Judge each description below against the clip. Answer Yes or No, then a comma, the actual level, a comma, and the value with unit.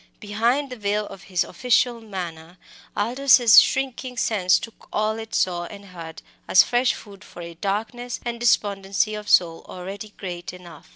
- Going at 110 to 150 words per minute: No, average, 160 wpm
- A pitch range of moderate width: Yes, average, 4.4 semitones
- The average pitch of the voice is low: No, high, 205 Hz